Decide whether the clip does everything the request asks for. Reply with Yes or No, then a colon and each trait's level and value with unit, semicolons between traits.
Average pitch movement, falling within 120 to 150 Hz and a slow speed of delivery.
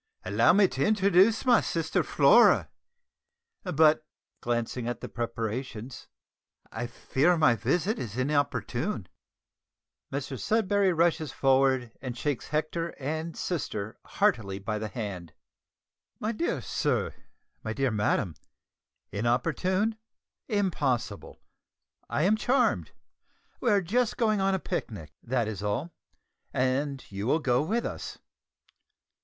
No: wide, 7.7 semitones; low, 135 Hz; slow, 120 wpm